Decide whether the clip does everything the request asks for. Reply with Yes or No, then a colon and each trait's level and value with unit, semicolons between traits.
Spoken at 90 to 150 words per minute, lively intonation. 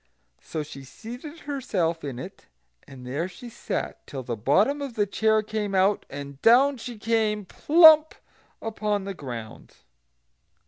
Yes: average, 145 wpm; wide, 8.8 semitones